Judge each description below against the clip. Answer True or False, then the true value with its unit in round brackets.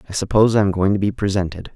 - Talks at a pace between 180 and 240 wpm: False (275 wpm)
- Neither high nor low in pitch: False (100 Hz)